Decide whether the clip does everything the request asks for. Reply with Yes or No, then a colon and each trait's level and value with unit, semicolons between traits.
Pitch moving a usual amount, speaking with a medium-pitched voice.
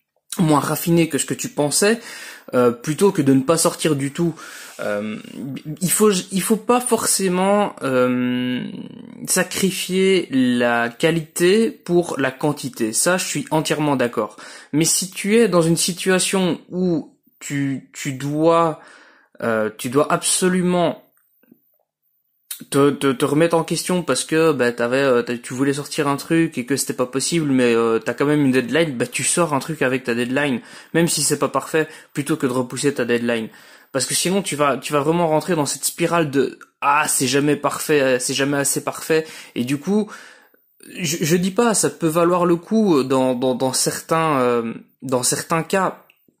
Yes: average, 4.8 semitones; medium, 155 Hz